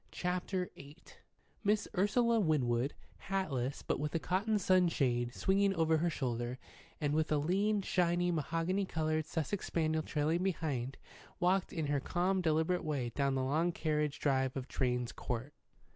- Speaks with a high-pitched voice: No, medium, 160 Hz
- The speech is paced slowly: No, average, 150 wpm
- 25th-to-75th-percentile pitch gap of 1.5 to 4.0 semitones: No, average, 4.7 semitones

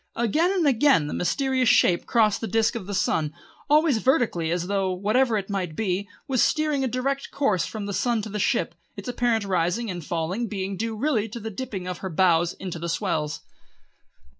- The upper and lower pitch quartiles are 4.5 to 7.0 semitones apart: Yes, average, 5.3 semitones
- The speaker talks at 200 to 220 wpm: Yes, fast, 205 wpm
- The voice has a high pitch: Yes, high, 210 Hz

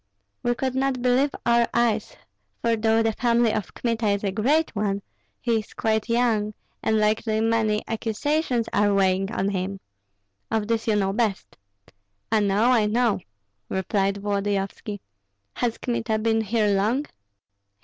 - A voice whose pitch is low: No, high, 220 Hz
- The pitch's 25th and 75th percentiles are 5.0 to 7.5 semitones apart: No, narrow, 2.5 semitones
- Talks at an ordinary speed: Yes, average, 150 wpm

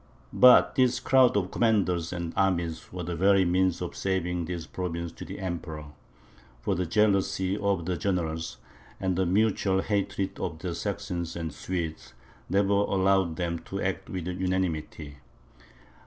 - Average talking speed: Yes, average, 155 wpm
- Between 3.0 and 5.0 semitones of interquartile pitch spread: No, narrow, 2.5 semitones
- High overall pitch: No, very low, 90 Hz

